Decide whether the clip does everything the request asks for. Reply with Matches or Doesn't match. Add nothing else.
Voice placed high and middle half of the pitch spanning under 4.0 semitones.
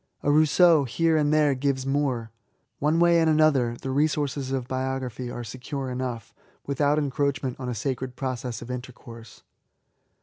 Doesn't match